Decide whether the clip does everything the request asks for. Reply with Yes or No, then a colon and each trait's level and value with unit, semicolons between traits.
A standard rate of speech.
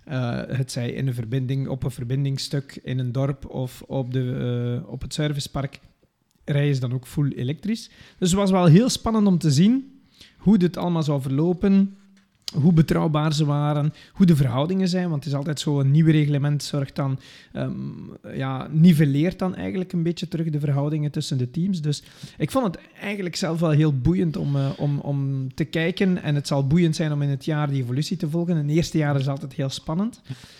No: fast, 210 wpm